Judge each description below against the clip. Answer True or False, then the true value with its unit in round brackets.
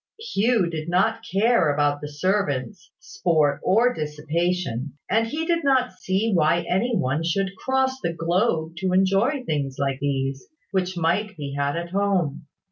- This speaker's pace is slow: False (155 wpm)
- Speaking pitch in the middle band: True (180 Hz)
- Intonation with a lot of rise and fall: True (6.0 semitones)